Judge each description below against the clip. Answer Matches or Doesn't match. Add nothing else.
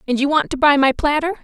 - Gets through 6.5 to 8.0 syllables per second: Matches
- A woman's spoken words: Matches